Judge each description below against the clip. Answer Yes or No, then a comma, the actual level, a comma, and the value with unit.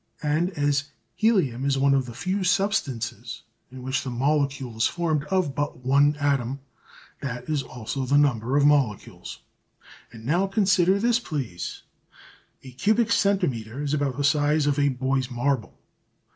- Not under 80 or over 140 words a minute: No, average, 155 wpm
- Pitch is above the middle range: No, medium, 140 Hz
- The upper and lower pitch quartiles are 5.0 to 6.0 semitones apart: No, average, 3.5 semitones